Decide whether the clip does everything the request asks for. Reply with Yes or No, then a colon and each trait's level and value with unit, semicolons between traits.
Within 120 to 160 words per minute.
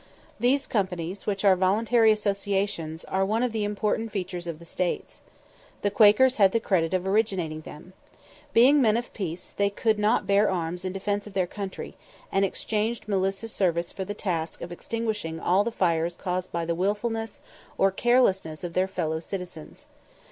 No: average, 175 wpm